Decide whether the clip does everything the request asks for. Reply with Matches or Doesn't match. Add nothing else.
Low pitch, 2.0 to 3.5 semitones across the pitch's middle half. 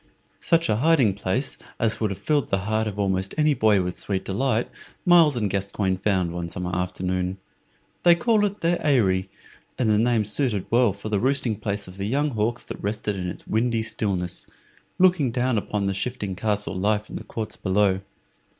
Doesn't match